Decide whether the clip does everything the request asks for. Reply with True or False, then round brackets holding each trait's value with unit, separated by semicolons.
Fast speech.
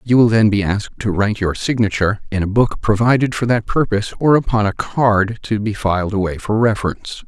True (215 wpm)